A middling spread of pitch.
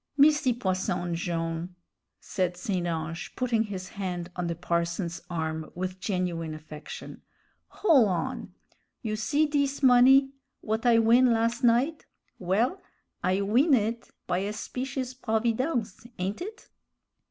No: wide, 6.0 semitones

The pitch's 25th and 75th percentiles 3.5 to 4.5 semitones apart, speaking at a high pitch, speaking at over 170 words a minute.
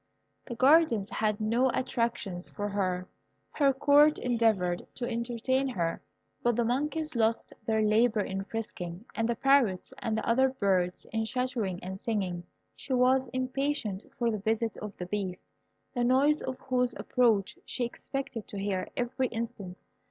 No: average, 4.1 semitones; high, 230 Hz; average, 150 wpm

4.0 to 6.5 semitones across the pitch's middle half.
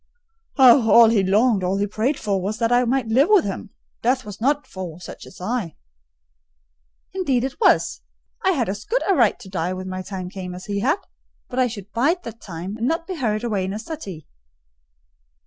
Yes: average, 5.2 semitones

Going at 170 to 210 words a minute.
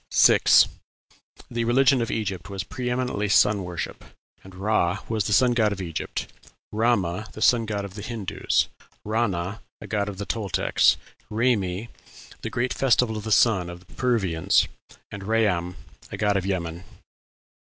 No: average, 155 wpm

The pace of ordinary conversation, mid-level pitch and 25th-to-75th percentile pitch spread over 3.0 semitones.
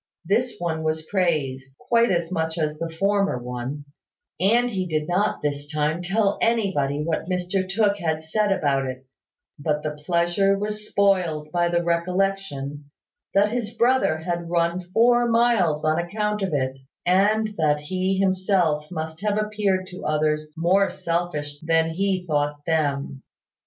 Yes: average, 150 wpm; medium, 175 Hz; average, 4.5 semitones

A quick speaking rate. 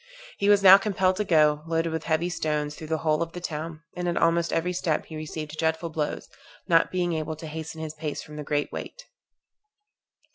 Yes: fast, 210 wpm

